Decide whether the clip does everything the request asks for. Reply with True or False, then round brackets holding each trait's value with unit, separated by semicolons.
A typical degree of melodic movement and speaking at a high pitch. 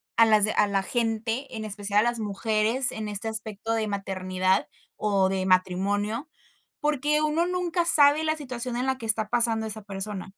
True (3.9 semitones; 220 Hz)